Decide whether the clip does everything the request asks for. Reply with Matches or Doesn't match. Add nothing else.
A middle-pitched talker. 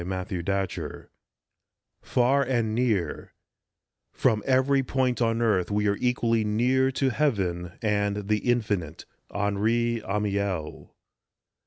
Doesn't match